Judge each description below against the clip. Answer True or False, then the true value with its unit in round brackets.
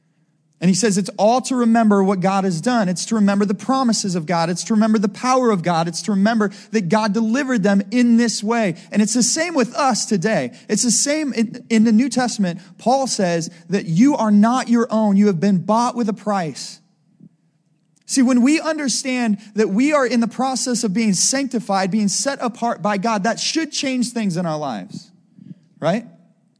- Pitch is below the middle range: False (220 Hz)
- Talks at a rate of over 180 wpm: True (205 wpm)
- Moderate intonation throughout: True (3.8 semitones)